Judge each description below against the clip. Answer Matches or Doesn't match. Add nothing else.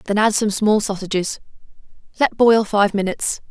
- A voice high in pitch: Matches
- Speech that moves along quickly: Doesn't match